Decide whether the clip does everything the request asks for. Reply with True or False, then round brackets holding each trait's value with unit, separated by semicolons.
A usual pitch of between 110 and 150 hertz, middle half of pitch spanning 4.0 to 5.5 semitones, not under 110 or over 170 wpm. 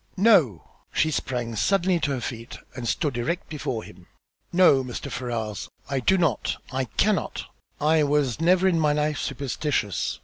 True (140 Hz; 5.1 semitones; 160 wpm)